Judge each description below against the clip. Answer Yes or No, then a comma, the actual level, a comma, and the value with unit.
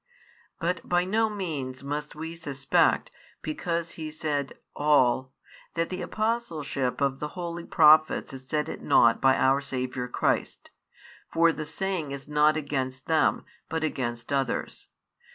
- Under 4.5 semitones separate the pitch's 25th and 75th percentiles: Yes, average, 3.7 semitones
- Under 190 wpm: Yes, average, 140 wpm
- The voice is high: No, medium, 150 Hz